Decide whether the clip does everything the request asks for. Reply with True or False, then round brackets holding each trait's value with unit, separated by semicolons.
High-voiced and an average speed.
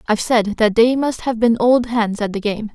False (225 Hz; 260 wpm)